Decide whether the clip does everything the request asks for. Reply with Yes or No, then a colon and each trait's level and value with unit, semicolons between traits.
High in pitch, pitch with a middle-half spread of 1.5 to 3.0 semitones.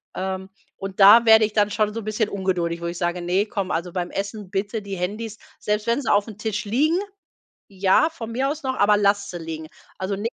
Yes: high, 205 Hz; average, 2.7 semitones